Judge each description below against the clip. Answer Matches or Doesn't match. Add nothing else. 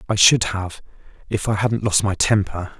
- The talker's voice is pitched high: Doesn't match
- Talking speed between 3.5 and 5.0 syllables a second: Matches